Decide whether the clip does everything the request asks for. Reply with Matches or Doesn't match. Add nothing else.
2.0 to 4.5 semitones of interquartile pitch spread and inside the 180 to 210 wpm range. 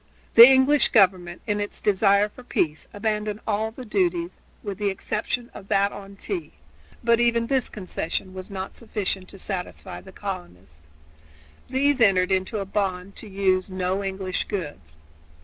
Doesn't match